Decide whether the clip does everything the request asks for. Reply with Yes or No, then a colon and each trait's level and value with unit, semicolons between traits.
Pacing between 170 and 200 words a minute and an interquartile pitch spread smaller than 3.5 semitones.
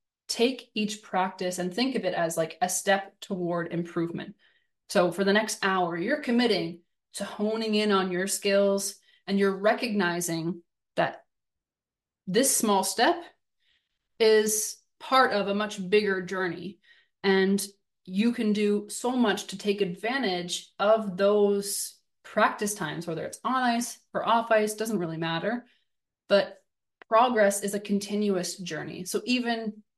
No: average, 140 wpm; average, 2.9 semitones